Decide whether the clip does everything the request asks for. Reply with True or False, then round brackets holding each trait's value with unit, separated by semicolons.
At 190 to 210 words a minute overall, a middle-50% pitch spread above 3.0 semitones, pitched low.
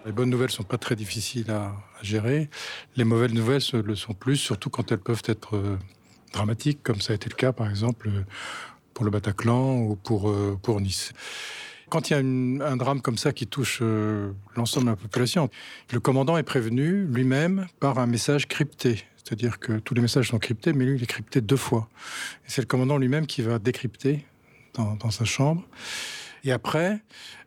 True (205 wpm; 3.7 semitones; 120 Hz)